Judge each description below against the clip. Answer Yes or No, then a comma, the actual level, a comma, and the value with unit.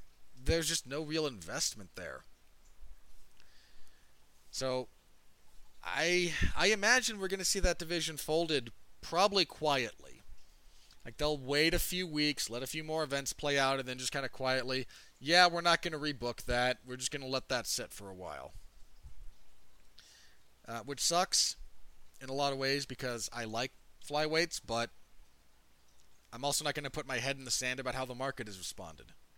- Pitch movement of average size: No, wide, 7.1 semitones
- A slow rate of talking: No, average, 175 wpm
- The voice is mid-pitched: No, low, 130 Hz